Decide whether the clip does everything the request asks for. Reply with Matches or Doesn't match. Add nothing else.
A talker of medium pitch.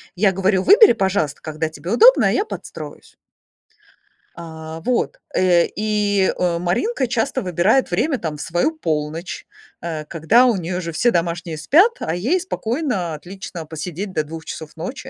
Matches